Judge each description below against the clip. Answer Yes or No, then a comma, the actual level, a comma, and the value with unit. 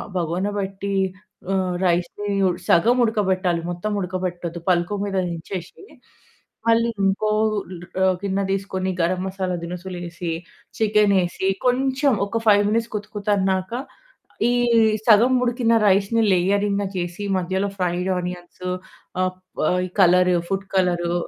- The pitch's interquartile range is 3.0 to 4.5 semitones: No, narrow, 2.4 semitones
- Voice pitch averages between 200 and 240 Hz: No, high, 190 Hz